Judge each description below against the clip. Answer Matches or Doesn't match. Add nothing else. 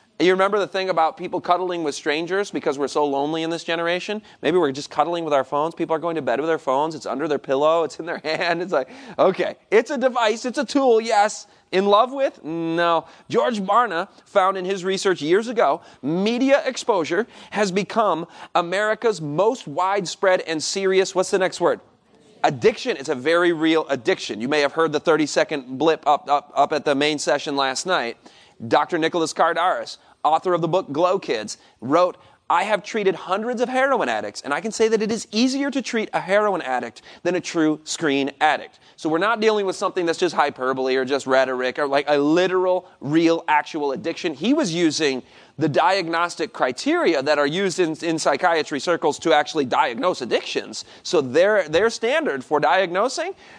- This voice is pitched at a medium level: Matches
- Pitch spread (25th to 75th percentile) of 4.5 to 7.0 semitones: Matches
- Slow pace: Doesn't match